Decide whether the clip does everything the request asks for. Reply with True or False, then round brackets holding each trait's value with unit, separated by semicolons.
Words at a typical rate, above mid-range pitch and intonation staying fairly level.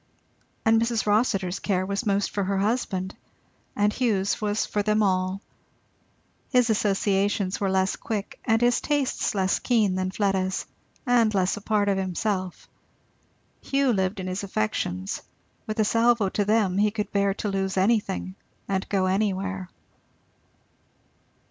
True (145 wpm; 200 Hz; 2.3 semitones)